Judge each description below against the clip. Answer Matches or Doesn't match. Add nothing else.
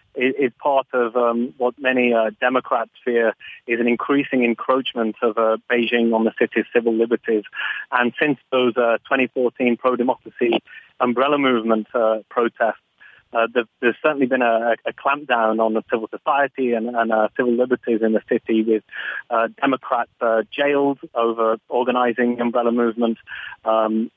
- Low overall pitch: Matches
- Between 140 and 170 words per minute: Matches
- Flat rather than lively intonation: Matches